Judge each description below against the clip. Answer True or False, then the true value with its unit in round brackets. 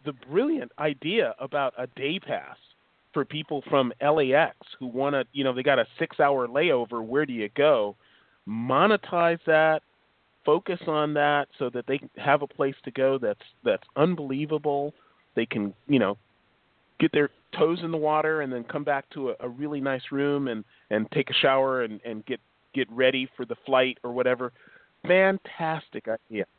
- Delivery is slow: False (180 wpm)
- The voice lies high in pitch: False (140 Hz)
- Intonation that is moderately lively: True (3.2 semitones)